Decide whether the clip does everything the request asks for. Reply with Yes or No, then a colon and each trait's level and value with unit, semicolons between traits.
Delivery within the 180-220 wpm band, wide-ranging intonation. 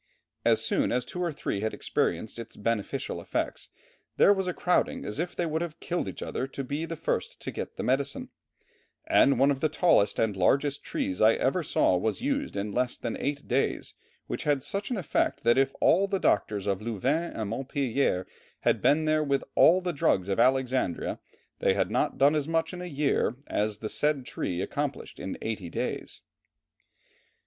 Yes: average, 195 wpm; wide, 6.3 semitones